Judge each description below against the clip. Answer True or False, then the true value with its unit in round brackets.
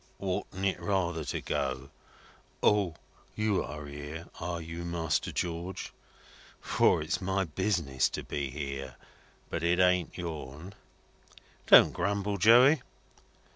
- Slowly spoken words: True (115 wpm)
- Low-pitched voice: True (85 Hz)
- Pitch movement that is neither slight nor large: True (4.1 semitones)